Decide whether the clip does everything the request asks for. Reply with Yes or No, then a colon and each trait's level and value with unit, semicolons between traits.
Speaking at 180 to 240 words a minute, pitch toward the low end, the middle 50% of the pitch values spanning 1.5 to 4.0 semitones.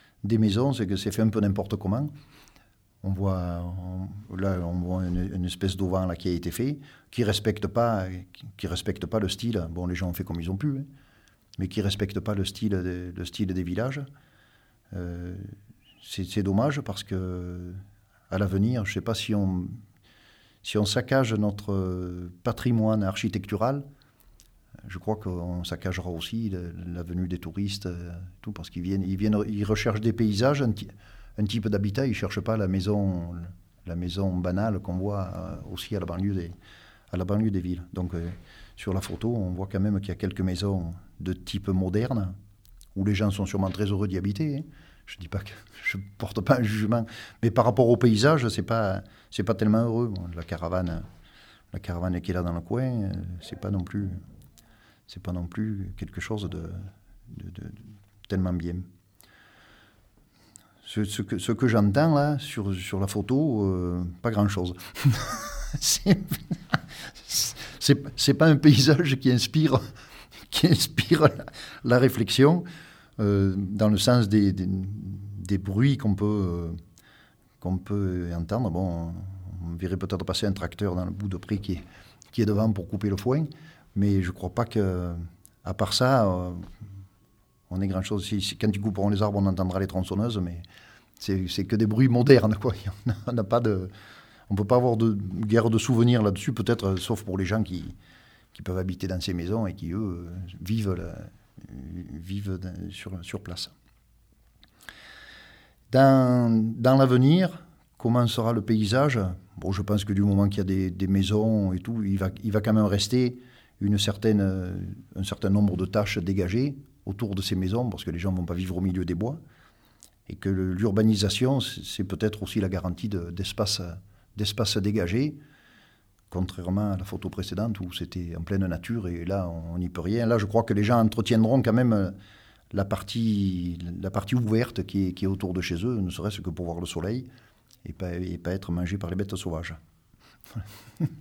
Yes: average, 185 wpm; low, 100 Hz; average, 3.3 semitones